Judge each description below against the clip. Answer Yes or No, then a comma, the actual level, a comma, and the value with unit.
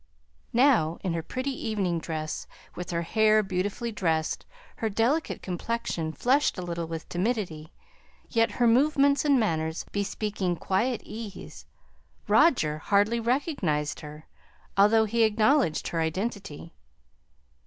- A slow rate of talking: Yes, slow, 120 wpm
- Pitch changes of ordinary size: No, wide, 5.8 semitones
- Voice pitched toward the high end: Yes, high, 205 Hz